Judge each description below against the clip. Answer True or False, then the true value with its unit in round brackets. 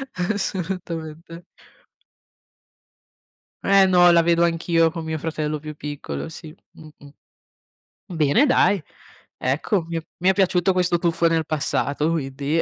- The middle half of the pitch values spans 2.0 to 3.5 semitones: True (2.6 semitones)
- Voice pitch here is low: False (165 Hz)